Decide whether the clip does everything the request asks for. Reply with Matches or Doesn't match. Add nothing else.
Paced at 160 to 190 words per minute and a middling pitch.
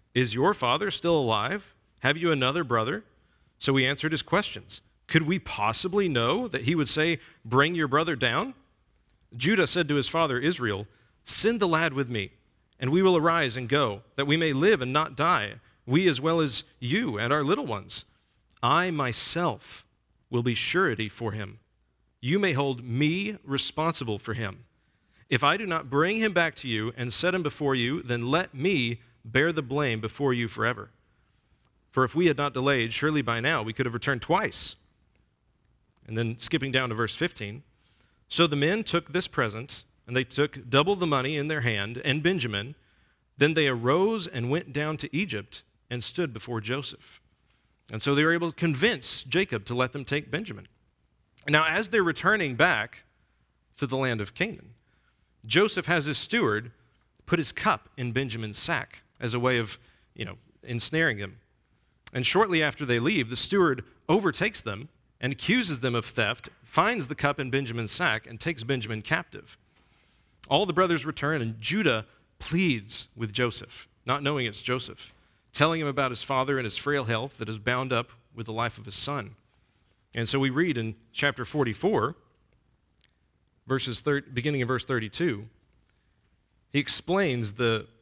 Doesn't match